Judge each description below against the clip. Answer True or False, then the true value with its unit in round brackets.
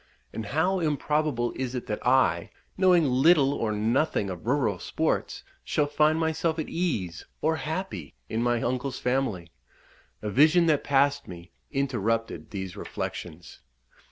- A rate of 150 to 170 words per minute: False (140 wpm)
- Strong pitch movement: True (6.1 semitones)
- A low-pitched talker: True (130 Hz)